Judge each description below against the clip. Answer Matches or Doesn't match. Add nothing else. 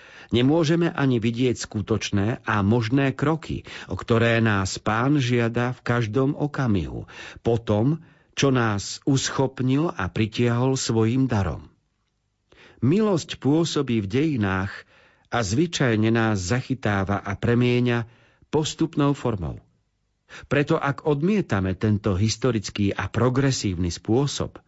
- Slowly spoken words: Matches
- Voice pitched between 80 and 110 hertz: Doesn't match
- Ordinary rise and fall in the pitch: Matches